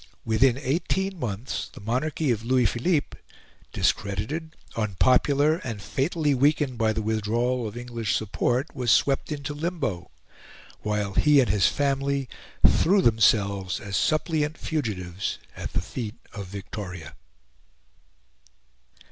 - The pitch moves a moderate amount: No, wide, 5.7 semitones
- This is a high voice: No, low, 120 Hz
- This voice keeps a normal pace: No, slow, 120 wpm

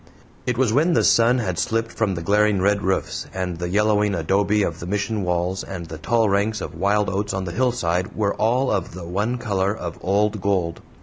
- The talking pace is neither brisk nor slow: No, fast, 210 wpm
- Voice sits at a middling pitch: No, low, 100 Hz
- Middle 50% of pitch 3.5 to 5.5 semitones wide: No, average, 3.0 semitones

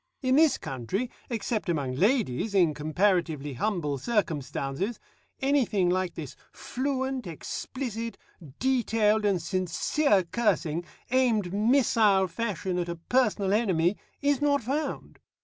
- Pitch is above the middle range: Yes, high, 205 Hz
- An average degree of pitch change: No, wide, 6.2 semitones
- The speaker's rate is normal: No, slow, 115 wpm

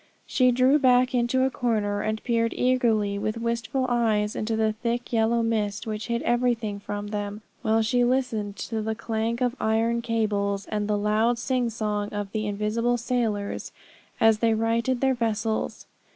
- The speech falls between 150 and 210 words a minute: Yes, average, 165 wpm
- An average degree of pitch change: No, narrow, 2.2 semitones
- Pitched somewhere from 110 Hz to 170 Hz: No, high, 225 Hz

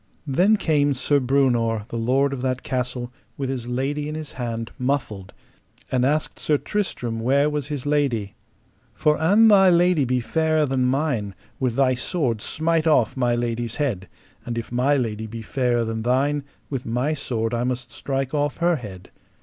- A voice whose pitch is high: No, low, 130 Hz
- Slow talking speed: No, average, 175 wpm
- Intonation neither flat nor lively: Yes, average, 3.6 semitones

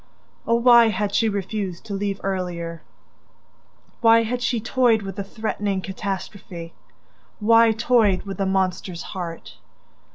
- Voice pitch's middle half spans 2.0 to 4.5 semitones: Yes, average, 3.2 semitones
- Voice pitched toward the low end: No, high, 200 Hz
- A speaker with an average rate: No, slow, 130 wpm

